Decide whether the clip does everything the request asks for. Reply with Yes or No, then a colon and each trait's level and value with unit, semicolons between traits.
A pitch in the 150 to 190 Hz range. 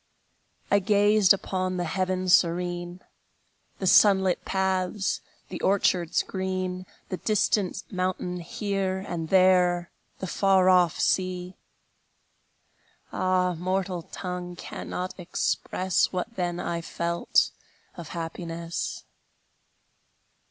Yes: medium, 185 Hz